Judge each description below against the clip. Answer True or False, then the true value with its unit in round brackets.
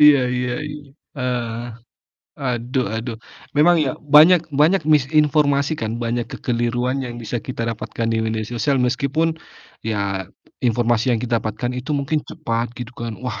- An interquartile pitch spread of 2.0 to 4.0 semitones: True (3.6 semitones)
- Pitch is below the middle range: True (125 Hz)